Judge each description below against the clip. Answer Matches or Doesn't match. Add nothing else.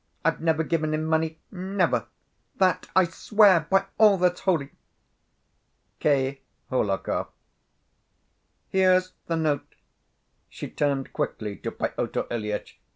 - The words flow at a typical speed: Doesn't match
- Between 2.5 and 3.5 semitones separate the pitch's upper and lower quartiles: Doesn't match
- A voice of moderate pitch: Matches